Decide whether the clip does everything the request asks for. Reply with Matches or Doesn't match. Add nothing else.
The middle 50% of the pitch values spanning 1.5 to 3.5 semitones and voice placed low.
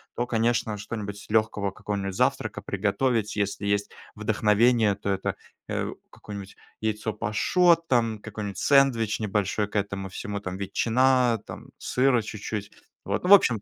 Matches